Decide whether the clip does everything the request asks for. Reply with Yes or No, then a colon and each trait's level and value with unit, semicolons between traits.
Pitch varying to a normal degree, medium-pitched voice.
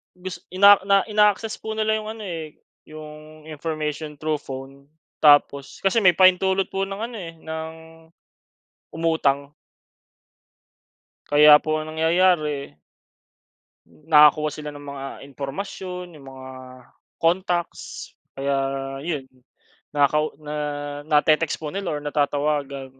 Yes: average, 3.9 semitones; medium, 155 Hz